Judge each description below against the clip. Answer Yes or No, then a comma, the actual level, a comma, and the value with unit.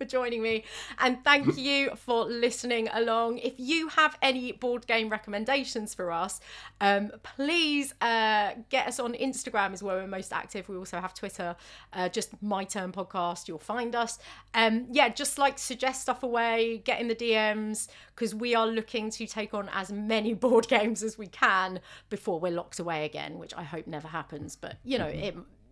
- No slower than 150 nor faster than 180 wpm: No, average, 190 wpm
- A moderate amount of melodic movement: Yes, average, 4.2 semitones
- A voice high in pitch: Yes, high, 225 Hz